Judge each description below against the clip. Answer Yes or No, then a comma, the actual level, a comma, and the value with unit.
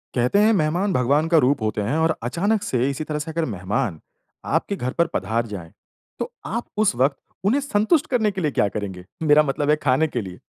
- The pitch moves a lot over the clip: Yes, wide, 7.5 semitones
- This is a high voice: No, medium, 150 Hz